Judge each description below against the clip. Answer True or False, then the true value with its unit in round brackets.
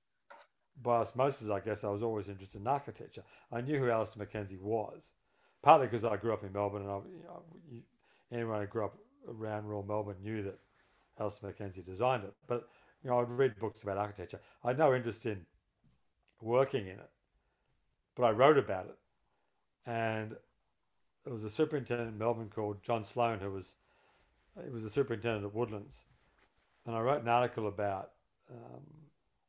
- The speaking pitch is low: True (115 Hz)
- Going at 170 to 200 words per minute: True (175 wpm)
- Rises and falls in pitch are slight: False (3.0 semitones)